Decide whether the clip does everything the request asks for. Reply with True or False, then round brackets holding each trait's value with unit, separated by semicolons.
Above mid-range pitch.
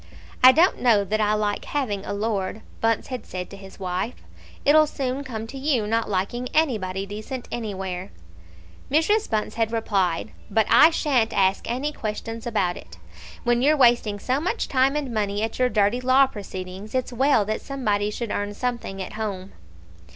True (220 Hz)